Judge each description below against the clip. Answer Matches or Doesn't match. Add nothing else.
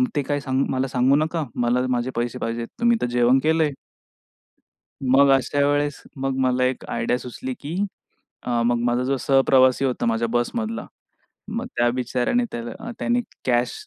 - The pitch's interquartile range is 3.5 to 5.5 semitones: Doesn't match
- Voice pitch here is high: Doesn't match